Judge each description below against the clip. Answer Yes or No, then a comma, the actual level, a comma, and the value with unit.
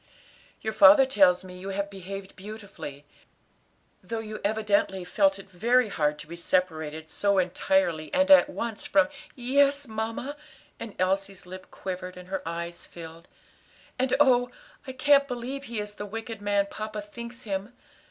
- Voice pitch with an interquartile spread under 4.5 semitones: No, average, 4.8 semitones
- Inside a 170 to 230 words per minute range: No, average, 160 wpm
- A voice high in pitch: Yes, high, 205 Hz